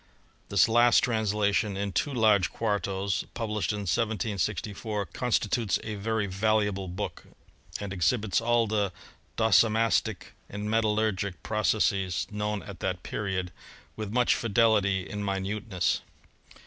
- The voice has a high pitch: No, low, 105 Hz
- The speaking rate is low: Yes, slow, 120 wpm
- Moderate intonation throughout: No, narrow, 2.1 semitones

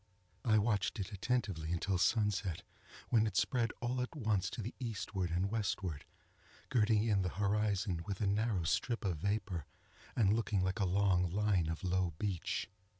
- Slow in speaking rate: No, average, 165 wpm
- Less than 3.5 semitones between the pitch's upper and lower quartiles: Yes, average, 3.0 semitones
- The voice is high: No, low, 100 Hz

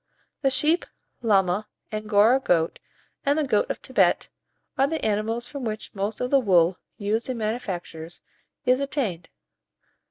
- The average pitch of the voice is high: Yes, high, 220 Hz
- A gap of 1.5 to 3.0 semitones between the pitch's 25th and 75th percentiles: No, average, 5.0 semitones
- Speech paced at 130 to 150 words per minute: Yes, average, 145 wpm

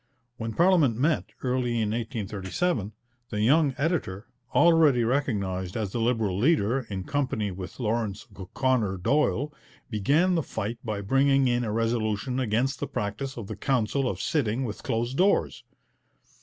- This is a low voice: Yes, low, 120 Hz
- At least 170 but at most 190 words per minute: No, average, 145 wpm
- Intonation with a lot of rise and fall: No, average, 4.5 semitones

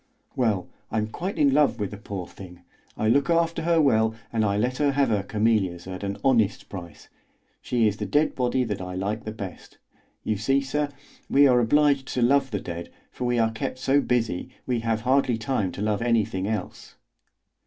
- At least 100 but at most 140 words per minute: No, average, 200 wpm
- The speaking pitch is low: Yes, low, 115 Hz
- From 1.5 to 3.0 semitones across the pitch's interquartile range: No, average, 4.8 semitones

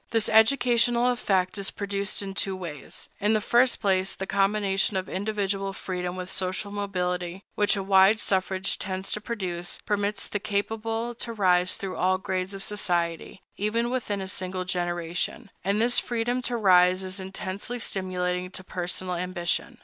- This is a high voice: Yes, high, 195 Hz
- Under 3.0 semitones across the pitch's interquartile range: Yes, narrow, 2.4 semitones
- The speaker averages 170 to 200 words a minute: No, average, 160 wpm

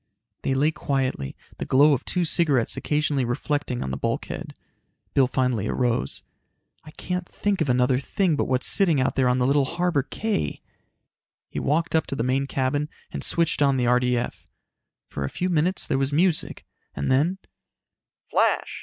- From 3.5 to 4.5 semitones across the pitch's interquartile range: Yes, average, 4.1 semitones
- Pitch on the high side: No, medium, 140 Hz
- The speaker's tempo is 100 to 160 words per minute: No, average, 170 wpm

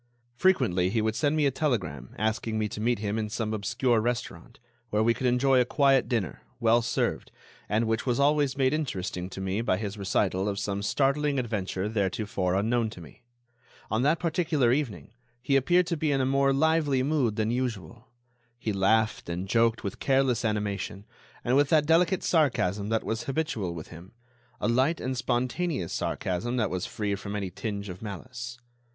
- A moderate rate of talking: Yes, average, 185 wpm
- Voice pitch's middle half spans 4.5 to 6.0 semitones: Yes, average, 4.9 semitones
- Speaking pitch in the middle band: No, low, 115 Hz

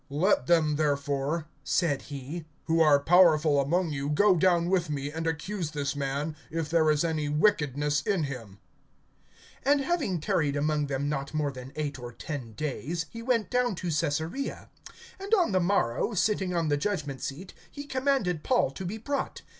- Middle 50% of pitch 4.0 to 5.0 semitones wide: Yes, average, 4.5 semitones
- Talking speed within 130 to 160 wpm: No, average, 175 wpm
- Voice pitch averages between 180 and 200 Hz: No, medium, 155 Hz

